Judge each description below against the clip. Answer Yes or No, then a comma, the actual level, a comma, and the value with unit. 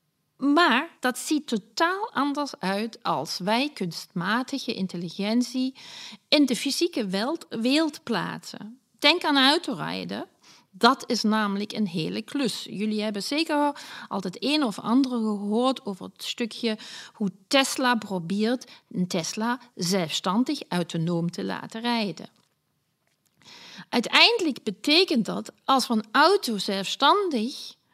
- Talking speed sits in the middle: No, slow, 120 wpm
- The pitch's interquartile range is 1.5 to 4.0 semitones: No, average, 5.2 semitones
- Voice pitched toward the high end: Yes, high, 235 Hz